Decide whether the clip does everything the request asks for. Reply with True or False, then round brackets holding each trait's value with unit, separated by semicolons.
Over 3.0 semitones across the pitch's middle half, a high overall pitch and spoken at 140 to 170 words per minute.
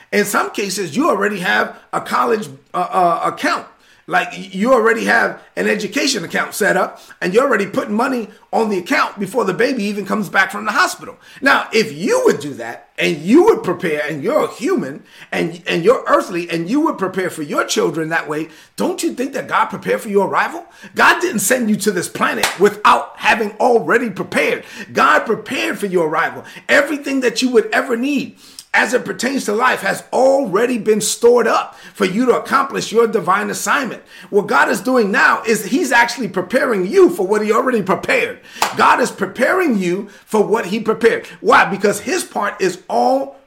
False (4.3 semitones; 225 Hz; 195 wpm)